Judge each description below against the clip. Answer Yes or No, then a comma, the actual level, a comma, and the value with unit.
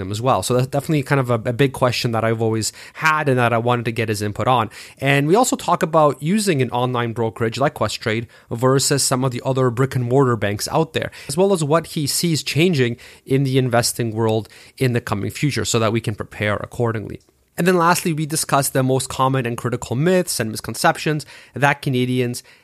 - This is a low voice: Yes, low, 130 Hz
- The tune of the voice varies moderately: Yes, average, 3.7 semitones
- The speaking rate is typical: No, fast, 215 wpm